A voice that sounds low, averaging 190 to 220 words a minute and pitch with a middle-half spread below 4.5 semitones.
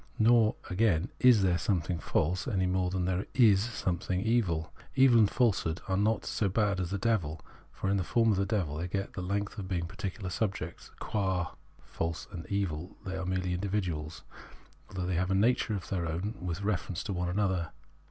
Yes: very low, 95 Hz; average, 200 wpm; average, 2.8 semitones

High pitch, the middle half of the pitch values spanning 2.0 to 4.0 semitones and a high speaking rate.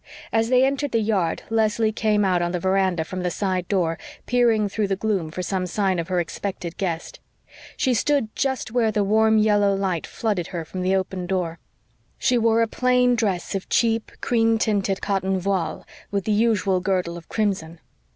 No: high, 200 Hz; average, 3.4 semitones; average, 190 wpm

